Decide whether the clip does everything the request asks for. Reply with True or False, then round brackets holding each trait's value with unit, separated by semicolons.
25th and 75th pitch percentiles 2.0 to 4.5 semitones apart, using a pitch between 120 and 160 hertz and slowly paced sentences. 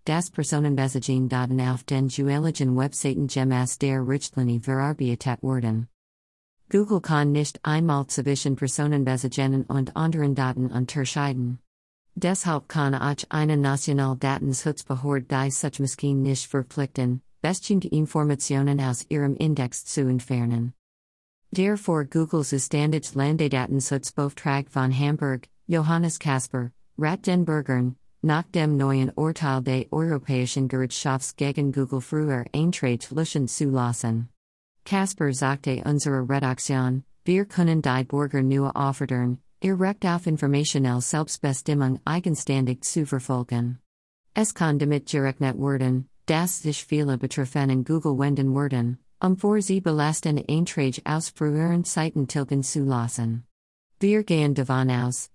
True (2.9 semitones; 140 Hz; 120 wpm)